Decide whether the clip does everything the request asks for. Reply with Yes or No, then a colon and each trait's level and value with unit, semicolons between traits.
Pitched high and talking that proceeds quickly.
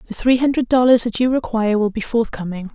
Yes: high, 230 Hz; fast, 220 wpm